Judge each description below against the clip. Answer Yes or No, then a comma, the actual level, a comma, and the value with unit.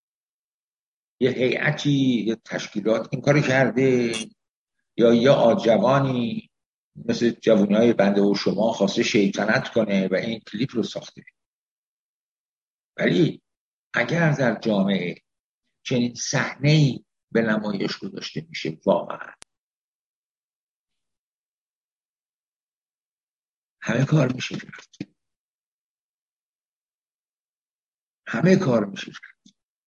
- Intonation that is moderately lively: Yes, average, 3.5 semitones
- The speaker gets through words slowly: Yes, slow, 85 wpm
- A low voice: Yes, low, 120 Hz